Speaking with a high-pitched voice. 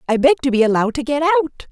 Yes: high, 240 Hz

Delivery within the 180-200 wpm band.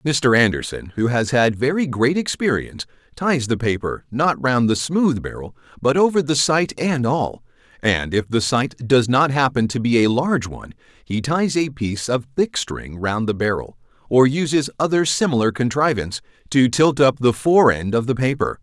Yes: average, 185 wpm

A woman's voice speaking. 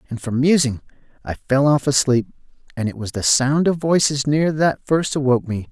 No: male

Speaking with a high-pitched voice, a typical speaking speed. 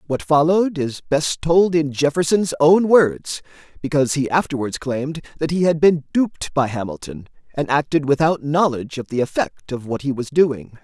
No: medium, 150 Hz; average, 175 wpm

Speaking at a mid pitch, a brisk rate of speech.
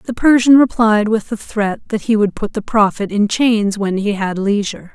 No: high, 215 Hz; fast, 220 wpm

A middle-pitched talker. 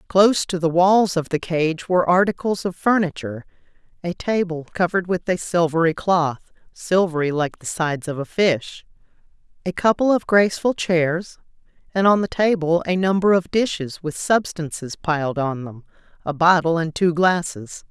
Yes: medium, 175 Hz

